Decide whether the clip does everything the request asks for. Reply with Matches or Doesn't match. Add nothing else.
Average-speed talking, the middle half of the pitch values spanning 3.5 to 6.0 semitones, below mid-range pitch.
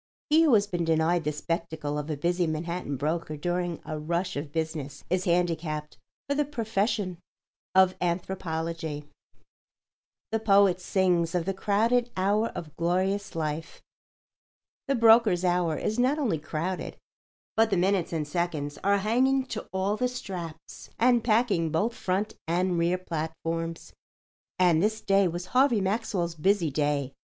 Doesn't match